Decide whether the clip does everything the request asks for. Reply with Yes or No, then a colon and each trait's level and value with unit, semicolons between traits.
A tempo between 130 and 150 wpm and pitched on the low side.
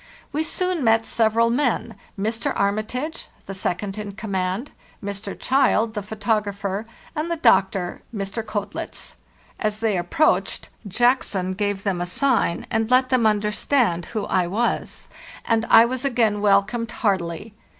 No: average, 140 wpm; high, 215 Hz